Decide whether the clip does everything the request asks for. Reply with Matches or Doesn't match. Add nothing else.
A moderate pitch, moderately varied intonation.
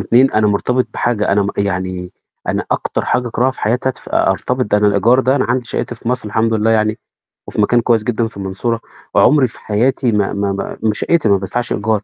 Doesn't match